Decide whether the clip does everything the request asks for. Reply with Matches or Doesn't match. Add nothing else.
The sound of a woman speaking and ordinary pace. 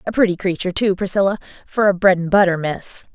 Doesn't match